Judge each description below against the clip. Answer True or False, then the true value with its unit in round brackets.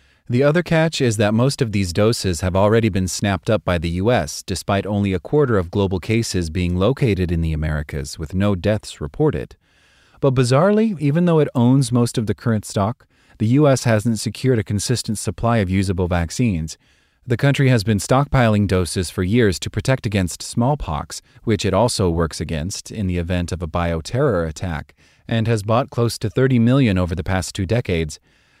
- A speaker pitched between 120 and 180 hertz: False (105 Hz)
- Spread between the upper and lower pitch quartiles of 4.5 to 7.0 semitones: True (5.1 semitones)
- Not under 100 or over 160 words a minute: False (190 wpm)